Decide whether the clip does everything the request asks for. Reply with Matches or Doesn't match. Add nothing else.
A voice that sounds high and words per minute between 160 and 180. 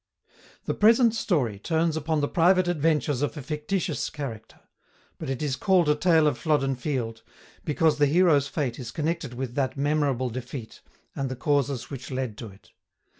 Doesn't match